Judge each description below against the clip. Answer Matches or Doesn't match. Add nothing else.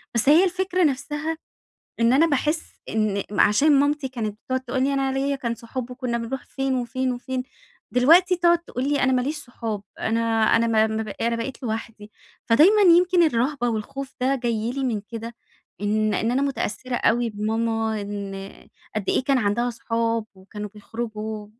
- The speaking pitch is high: Matches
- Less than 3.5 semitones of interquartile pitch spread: Doesn't match